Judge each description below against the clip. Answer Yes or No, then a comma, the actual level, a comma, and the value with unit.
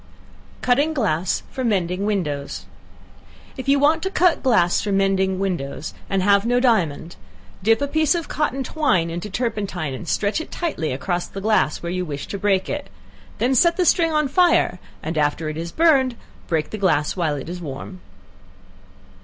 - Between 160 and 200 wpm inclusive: Yes, average, 180 wpm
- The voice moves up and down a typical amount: No, wide, 7.8 semitones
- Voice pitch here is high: Yes, high, 195 Hz